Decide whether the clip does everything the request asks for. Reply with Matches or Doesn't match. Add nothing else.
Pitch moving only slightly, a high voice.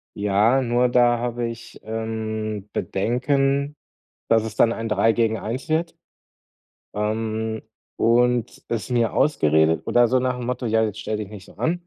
Doesn't match